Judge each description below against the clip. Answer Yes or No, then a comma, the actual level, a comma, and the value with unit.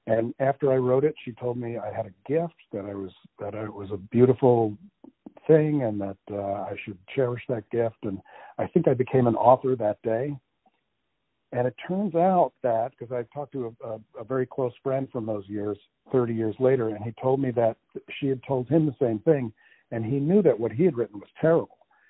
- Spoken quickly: Yes, fast, 225 wpm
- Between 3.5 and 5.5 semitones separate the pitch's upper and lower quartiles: Yes, average, 3.9 semitones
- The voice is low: Yes, low, 125 Hz